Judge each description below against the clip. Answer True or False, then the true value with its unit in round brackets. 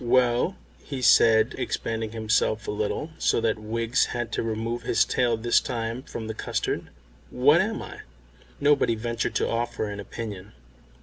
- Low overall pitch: True (115 Hz)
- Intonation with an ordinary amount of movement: False (1.7 semitones)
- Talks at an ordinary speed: True (160 wpm)